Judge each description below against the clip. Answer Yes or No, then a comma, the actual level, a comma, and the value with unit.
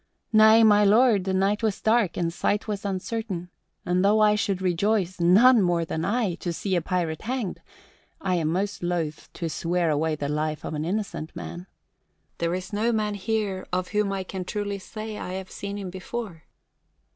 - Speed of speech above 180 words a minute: Yes, average, 190 wpm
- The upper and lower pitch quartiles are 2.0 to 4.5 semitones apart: Yes, average, 3.2 semitones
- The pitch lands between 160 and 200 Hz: Yes, high, 190 Hz